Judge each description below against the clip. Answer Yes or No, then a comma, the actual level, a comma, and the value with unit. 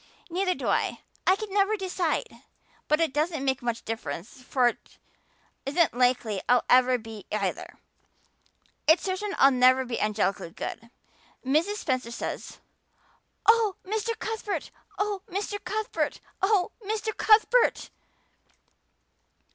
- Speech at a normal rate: No, slow, 125 wpm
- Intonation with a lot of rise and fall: Yes, wide, 8.6 semitones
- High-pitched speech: Yes, very high, 320 Hz